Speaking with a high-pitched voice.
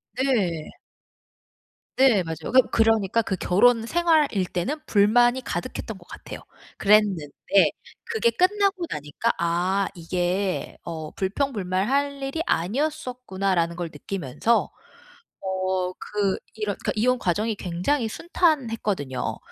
Yes: high, 205 Hz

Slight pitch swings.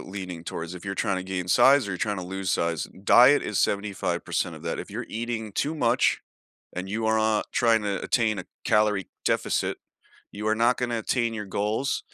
No: average, 3.3 semitones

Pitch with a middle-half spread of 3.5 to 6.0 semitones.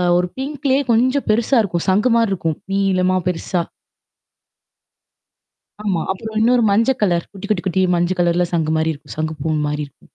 Yes: average, 4.7 semitones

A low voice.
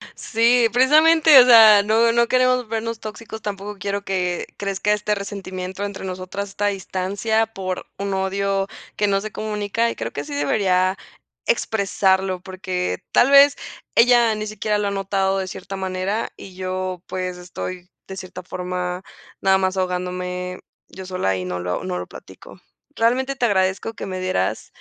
No: high, 195 Hz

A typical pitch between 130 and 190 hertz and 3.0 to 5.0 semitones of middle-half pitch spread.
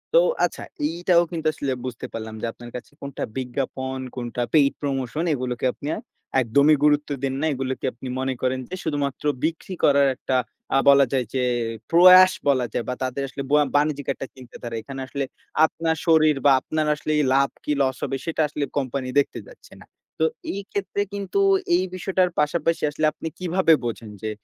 Yes: medium, 140 Hz; average, 3.7 semitones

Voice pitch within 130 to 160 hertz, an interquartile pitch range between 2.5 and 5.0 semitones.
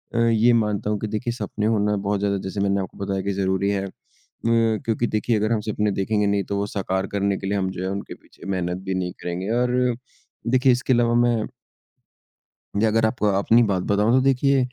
No: low, 105 Hz; average, 2.9 semitones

